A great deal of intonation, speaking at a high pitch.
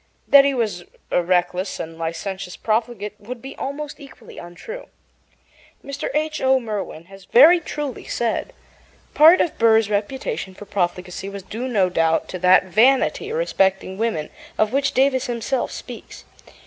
Yes: wide, 6.4 semitones; high, 220 Hz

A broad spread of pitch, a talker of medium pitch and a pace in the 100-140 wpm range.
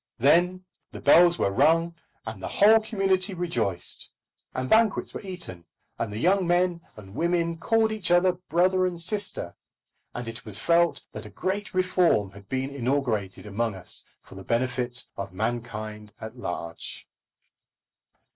No: wide, 8.7 semitones; medium, 155 Hz; average, 150 wpm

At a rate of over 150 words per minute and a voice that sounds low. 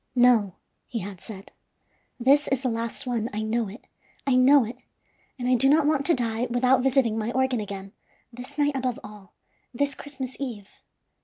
No: average, 180 wpm; high, 245 Hz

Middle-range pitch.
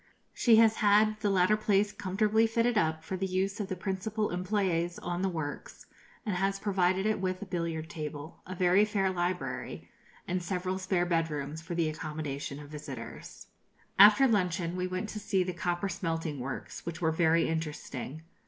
Yes: medium, 180 Hz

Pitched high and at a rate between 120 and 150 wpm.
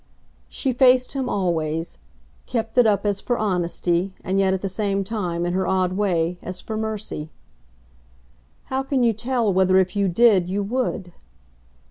No: high, 195 Hz; average, 165 wpm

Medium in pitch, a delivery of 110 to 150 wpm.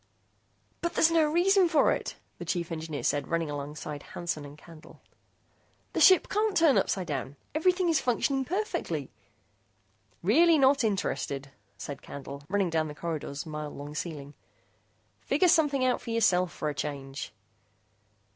Yes: medium, 175 Hz; average, 145 wpm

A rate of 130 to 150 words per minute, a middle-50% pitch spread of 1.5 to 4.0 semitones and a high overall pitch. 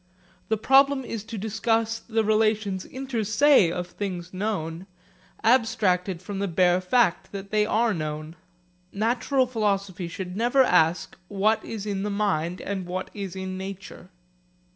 Yes: average, 145 wpm; average, 3.4 semitones; high, 200 Hz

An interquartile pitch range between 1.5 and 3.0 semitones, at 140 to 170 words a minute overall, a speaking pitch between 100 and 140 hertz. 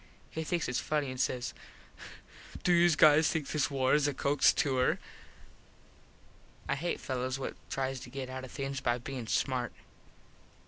Yes: narrow, 2.5 semitones; average, 165 wpm; low, 135 Hz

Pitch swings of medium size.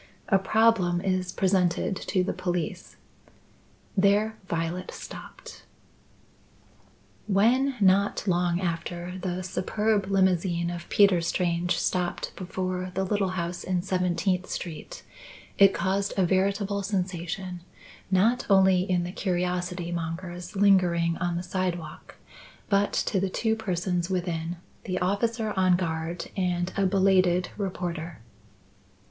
No: narrow, 1.9 semitones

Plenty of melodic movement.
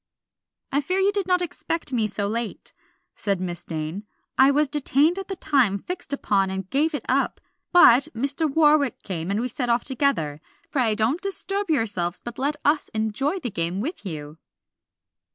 Yes: wide, 7.3 semitones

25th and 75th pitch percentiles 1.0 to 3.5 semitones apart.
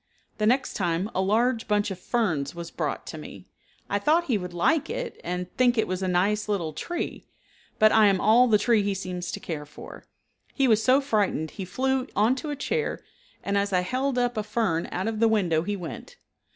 No: average, 5.3 semitones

